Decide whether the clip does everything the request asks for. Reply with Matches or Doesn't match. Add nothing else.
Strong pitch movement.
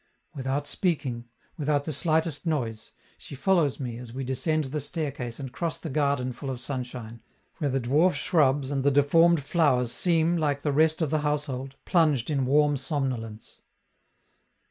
Doesn't match